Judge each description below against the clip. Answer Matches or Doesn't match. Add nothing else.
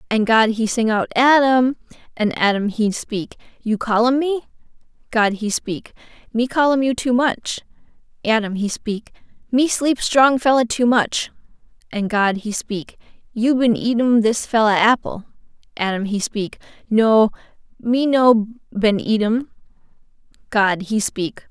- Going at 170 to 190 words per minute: Doesn't match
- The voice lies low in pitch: Doesn't match